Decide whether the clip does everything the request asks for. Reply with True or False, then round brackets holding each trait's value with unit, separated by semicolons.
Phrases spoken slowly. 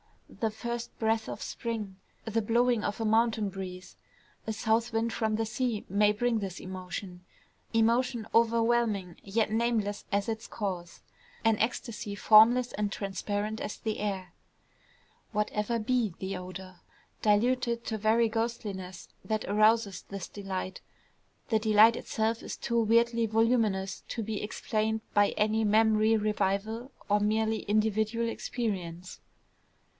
True (130 wpm)